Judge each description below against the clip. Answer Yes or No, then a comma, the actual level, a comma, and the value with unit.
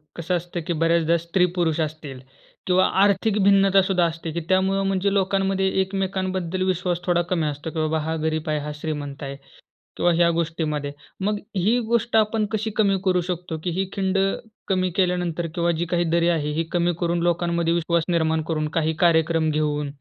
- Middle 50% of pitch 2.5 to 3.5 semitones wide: Yes, average, 2.8 semitones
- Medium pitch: Yes, medium, 170 Hz